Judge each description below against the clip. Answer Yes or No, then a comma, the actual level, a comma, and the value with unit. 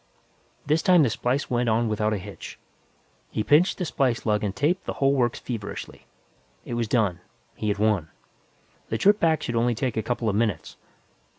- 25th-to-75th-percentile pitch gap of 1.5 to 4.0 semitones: No, average, 4.4 semitones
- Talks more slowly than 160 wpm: No, average, 190 wpm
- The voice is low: Yes, low, 120 Hz